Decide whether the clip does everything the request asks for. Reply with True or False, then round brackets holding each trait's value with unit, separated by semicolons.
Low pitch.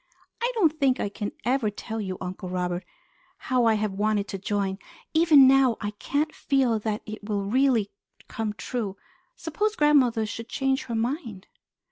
False (225 Hz)